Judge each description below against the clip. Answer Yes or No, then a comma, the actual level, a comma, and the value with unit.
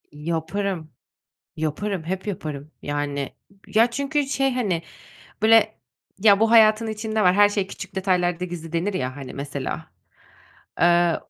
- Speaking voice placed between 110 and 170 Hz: No, medium, 185 Hz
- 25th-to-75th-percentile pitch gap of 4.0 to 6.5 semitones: Yes, average, 5.3 semitones